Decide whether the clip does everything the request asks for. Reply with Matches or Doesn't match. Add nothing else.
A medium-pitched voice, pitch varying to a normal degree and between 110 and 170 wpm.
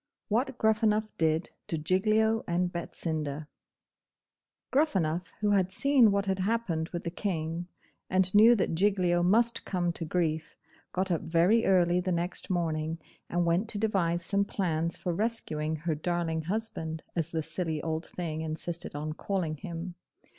Matches